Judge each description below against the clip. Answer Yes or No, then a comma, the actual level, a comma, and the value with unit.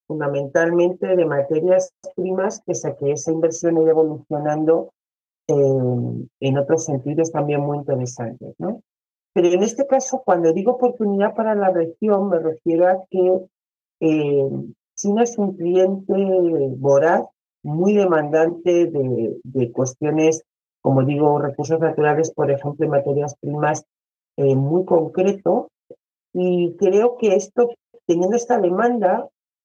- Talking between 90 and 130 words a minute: Yes, slow, 125 wpm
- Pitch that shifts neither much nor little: Yes, average, 4.3 semitones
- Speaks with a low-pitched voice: No, medium, 165 Hz